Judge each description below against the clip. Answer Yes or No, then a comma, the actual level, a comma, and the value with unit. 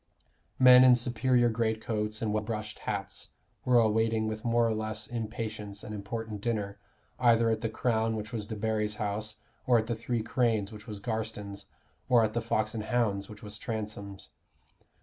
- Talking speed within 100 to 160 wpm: No, average, 170 wpm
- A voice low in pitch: Yes, low, 110 Hz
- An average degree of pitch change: No, narrow, 1.6 semitones